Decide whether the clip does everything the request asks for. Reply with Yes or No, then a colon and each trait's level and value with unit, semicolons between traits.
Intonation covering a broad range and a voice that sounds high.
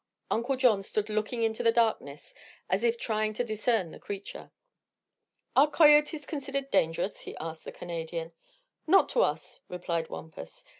Yes: wide, 6.7 semitones; high, 215 Hz